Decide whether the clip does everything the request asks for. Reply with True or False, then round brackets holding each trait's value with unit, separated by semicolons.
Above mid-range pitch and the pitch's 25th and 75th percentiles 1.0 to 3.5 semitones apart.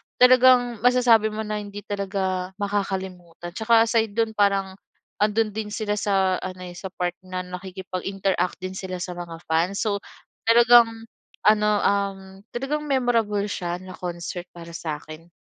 True (200 Hz; 3.2 semitones)